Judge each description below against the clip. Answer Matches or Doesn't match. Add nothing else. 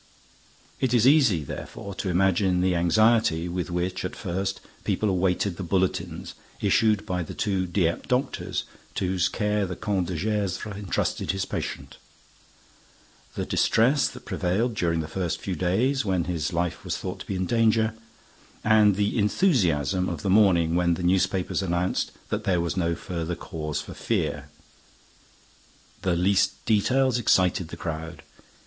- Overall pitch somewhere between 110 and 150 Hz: Doesn't match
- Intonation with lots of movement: Doesn't match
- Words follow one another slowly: Doesn't match